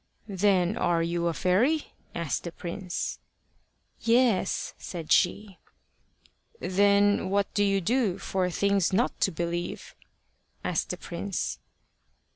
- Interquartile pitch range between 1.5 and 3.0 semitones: Yes, average, 2.7 semitones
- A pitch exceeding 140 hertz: Yes, high, 190 Hz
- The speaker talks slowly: Yes, slow, 115 wpm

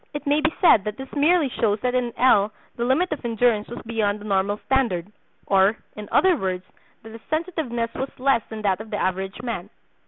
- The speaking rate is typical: No, fast, 210 wpm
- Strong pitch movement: No, average, 4.5 semitones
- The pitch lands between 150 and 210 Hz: No, high, 230 Hz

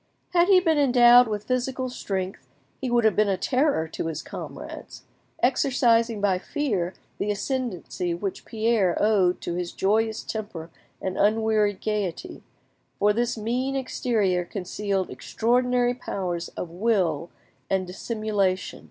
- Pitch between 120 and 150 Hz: No, high, 215 Hz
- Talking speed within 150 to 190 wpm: No, slow, 135 wpm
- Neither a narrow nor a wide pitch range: Yes, average, 4.6 semitones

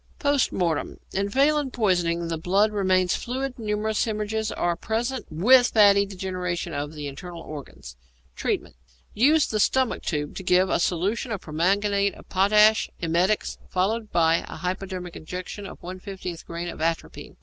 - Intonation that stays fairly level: No, average, 3.9 semitones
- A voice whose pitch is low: No, high, 190 Hz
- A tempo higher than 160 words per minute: No, average, 150 wpm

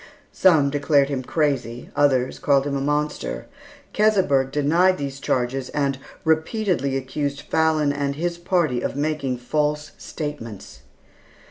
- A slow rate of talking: Yes, slow, 125 wpm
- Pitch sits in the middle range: Yes, medium, 145 Hz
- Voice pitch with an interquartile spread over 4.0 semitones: No, narrow, 2.6 semitones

